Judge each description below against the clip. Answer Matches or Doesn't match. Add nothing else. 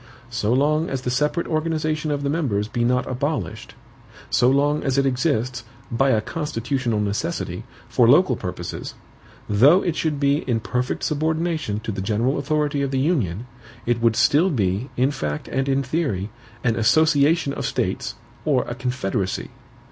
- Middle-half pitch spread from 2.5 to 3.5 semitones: Doesn't match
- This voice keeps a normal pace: Matches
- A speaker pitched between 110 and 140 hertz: Matches